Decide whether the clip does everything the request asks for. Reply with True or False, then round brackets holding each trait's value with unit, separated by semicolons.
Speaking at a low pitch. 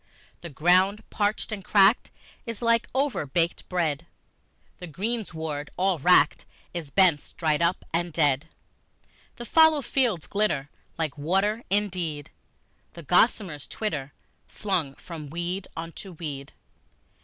False (175 Hz)